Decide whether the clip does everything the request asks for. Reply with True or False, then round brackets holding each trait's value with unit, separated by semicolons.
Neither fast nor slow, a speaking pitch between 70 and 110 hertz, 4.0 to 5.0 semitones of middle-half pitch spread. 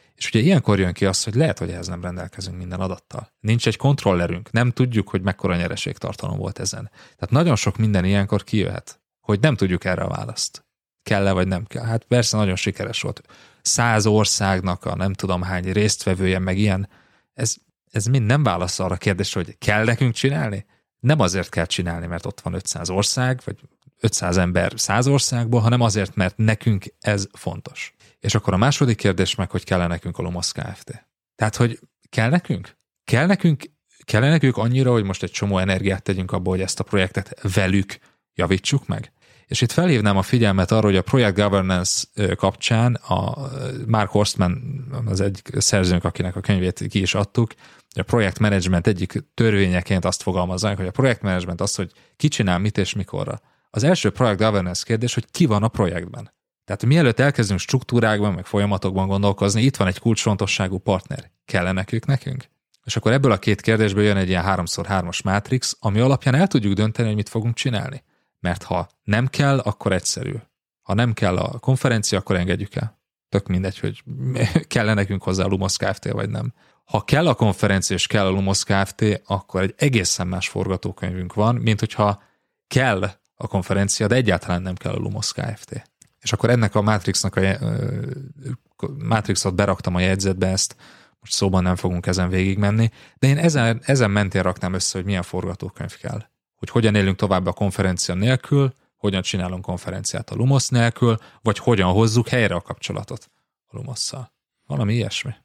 False (180 wpm; 105 Hz; 4.4 semitones)